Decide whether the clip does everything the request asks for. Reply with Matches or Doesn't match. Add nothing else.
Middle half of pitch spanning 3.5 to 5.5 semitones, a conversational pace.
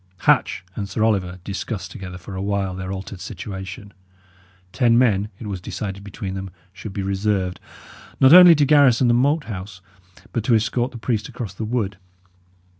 Matches